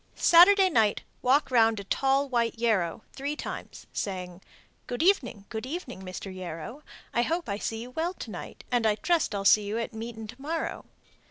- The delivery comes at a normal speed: Yes, average, 180 wpm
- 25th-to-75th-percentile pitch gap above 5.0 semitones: Yes, wide, 5.4 semitones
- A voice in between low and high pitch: No, high, 235 Hz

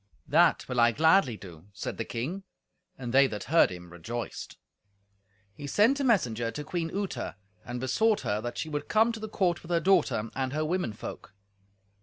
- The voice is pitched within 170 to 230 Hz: No, medium, 140 Hz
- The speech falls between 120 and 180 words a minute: No, average, 190 wpm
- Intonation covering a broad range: Yes, wide, 7.7 semitones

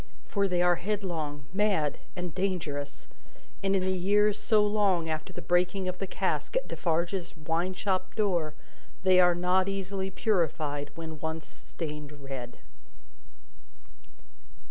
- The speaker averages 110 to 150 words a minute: Yes, slow, 135 wpm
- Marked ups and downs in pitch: No, average, 3.4 semitones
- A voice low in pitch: No, medium, 180 Hz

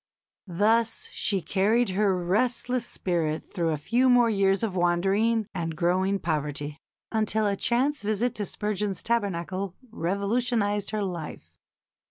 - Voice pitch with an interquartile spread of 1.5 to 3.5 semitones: No, average, 4.1 semitones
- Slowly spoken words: Yes, slow, 130 wpm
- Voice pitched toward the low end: No, high, 200 Hz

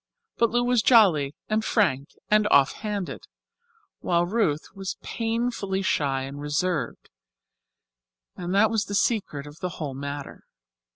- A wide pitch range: Yes, wide, 7.0 semitones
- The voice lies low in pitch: No, medium, 185 Hz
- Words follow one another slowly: Yes, slow, 130 wpm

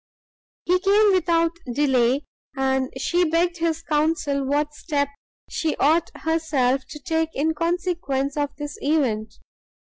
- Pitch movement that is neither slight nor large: Yes, average, 3.2 semitones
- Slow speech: Yes, slow, 125 wpm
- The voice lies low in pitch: No, very high, 305 Hz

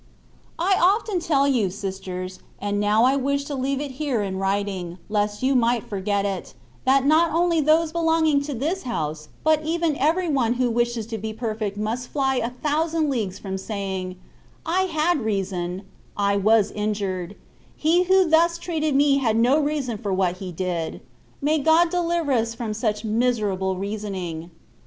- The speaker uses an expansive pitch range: Yes, wide, 7.3 semitones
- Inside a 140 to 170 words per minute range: No, average, 180 wpm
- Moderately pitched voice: No, high, 235 Hz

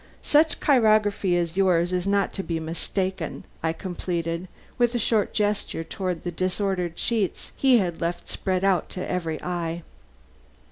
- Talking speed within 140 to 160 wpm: Yes, average, 150 wpm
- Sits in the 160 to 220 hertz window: Yes, medium, 185 Hz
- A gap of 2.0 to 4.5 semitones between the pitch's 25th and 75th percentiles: Yes, average, 3.0 semitones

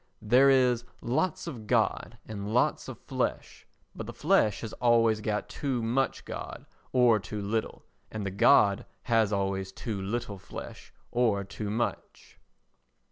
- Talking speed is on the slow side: No, average, 145 wpm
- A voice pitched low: Yes, low, 110 Hz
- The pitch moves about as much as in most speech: Yes, average, 3.1 semitones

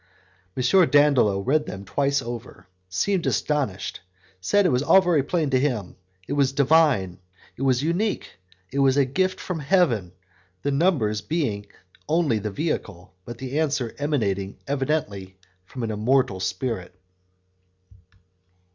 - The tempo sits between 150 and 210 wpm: No, average, 140 wpm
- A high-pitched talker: No, low, 135 Hz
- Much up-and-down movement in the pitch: Yes, wide, 6.3 semitones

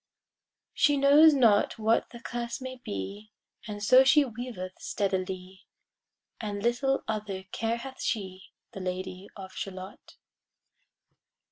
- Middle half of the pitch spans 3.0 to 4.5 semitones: No, average, 4.9 semitones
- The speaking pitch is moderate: No, high, 215 Hz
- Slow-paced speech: Yes, slow, 120 wpm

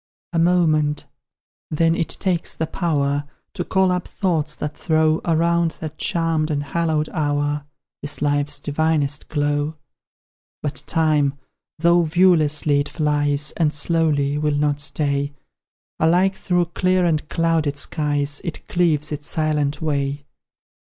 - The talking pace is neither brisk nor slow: No, slow, 130 wpm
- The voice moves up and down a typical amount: No, narrow, 2.3 semitones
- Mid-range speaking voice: Yes, medium, 155 Hz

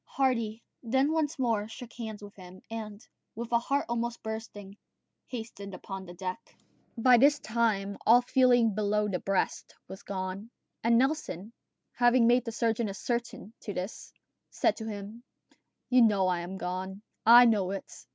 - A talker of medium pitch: No, high, 220 Hz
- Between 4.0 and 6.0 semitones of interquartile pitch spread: No, average, 3.2 semitones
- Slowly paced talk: No, average, 150 wpm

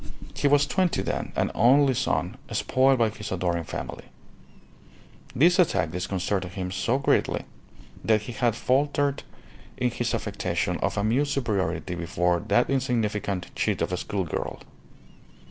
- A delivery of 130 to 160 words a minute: Yes, average, 140 wpm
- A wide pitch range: Yes, wide, 6.4 semitones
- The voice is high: No, low, 110 Hz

